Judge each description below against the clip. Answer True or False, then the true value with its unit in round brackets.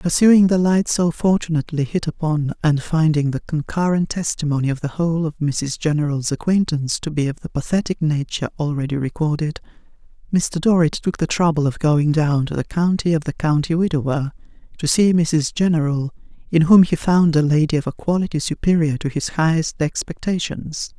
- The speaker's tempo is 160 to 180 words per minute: True (170 wpm)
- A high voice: False (160 Hz)